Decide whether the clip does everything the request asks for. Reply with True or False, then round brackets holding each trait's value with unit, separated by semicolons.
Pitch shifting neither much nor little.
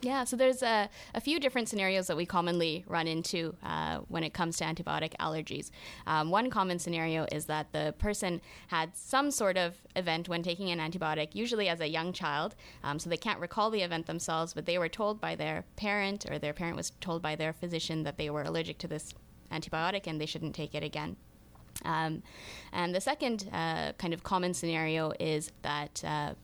True (3.3 semitones)